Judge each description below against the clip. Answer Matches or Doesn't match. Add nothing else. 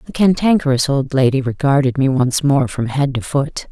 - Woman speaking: Matches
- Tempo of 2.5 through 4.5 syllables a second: Doesn't match